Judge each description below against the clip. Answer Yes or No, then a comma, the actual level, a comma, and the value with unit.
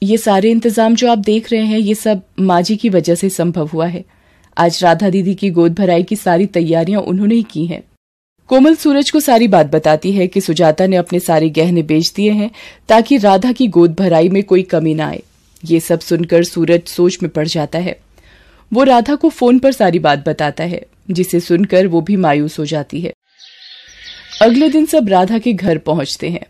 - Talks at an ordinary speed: No, fast, 205 wpm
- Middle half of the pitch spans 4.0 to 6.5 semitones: Yes, average, 5.1 semitones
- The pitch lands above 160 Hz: Yes, medium, 185 Hz